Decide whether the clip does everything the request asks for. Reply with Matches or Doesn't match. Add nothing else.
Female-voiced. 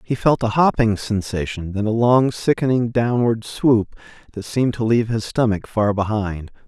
Doesn't match